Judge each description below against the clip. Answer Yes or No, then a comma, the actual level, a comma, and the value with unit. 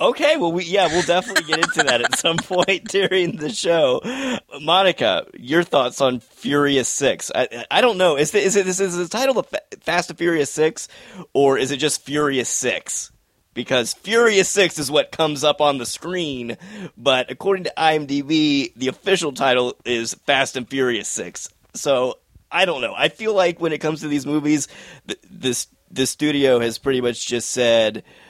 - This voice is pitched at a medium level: Yes, medium, 150 Hz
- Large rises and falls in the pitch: Yes, wide, 5.7 semitones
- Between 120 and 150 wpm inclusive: No, average, 185 wpm